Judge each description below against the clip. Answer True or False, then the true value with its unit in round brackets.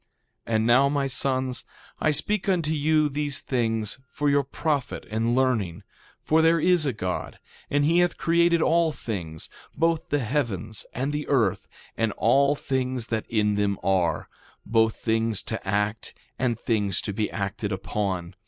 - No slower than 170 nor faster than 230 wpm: False (160 wpm)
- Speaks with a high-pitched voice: False (125 Hz)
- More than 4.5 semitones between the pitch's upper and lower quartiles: True (5.6 semitones)